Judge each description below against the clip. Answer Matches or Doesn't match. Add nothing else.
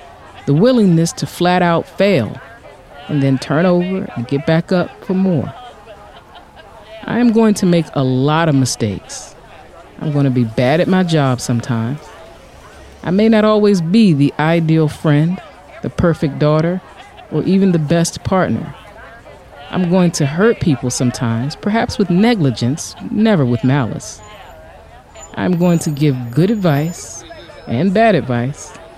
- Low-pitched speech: Doesn't match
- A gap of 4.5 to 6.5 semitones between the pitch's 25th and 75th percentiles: Matches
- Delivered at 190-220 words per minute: Doesn't match